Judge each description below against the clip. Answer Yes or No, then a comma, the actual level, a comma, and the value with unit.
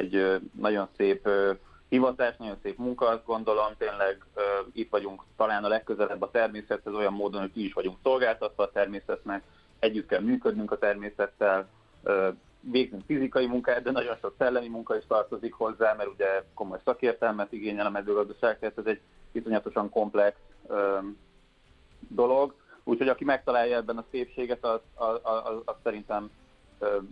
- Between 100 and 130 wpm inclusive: No, average, 145 wpm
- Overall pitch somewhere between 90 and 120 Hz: Yes, low, 105 Hz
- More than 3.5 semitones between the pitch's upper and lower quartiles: No, narrow, 2.6 semitones